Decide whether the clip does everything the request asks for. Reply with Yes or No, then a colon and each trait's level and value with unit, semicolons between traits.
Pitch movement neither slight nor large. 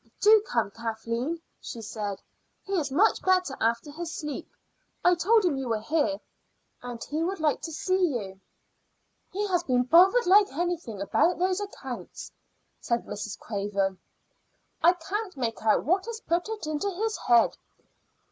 No: wide, 8.1 semitones